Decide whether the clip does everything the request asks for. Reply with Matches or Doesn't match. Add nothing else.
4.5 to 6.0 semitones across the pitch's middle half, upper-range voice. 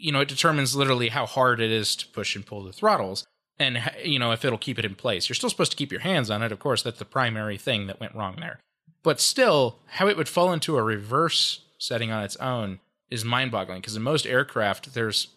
Doesn't match